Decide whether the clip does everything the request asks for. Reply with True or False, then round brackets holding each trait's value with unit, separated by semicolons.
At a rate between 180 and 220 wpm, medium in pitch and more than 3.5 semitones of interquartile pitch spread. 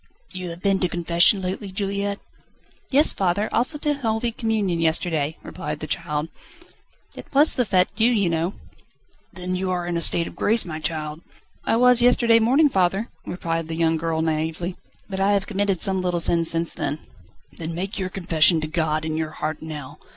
True (190 wpm; 180 Hz; 3.9 semitones)